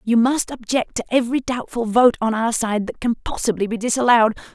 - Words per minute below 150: No, average, 200 wpm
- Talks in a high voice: Yes, high, 230 Hz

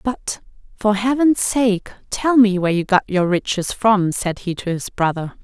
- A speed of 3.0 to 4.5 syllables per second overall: Yes, 4.4 syllables/s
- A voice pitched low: No, high, 205 Hz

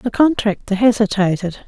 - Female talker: Yes, female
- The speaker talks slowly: Yes, slow, 110 wpm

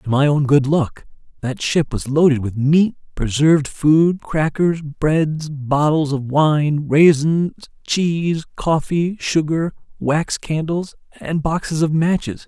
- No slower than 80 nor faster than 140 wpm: Yes, slow, 135 wpm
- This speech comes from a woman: No, male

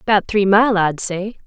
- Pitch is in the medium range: No, high, 200 Hz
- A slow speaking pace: No, fast, 205 wpm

